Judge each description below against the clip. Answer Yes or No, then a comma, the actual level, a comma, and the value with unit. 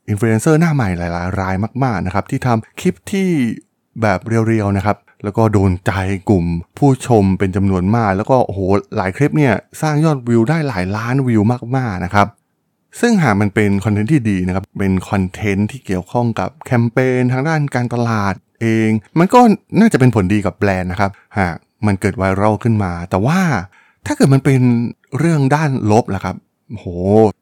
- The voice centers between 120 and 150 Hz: No, low, 110 Hz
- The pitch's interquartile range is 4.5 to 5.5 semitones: Yes, average, 5.1 semitones